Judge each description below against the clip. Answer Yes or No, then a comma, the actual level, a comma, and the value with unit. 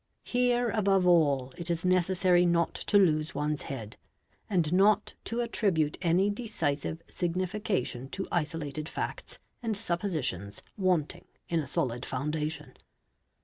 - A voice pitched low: No, medium, 170 Hz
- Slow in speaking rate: Yes, slow, 125 wpm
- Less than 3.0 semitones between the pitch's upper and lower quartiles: No, average, 4.4 semitones